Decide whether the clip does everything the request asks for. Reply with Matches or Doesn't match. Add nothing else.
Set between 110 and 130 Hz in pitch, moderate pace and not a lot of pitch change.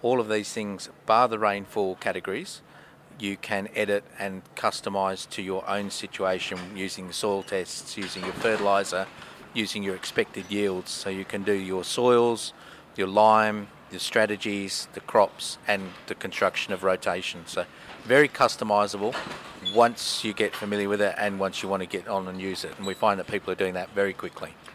Doesn't match